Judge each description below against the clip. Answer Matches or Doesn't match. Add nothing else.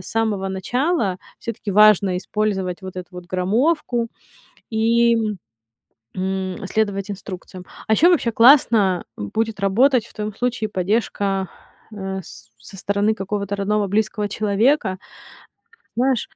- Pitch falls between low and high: Doesn't match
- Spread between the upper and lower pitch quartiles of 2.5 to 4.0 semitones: Matches